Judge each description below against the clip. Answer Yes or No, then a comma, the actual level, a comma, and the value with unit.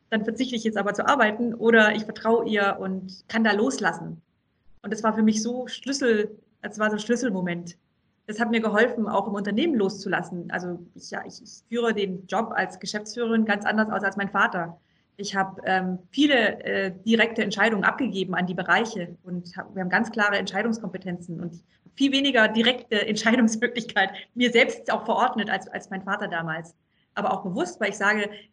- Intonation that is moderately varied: Yes, average, 3.1 semitones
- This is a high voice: Yes, high, 210 Hz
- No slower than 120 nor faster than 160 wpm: No, average, 185 wpm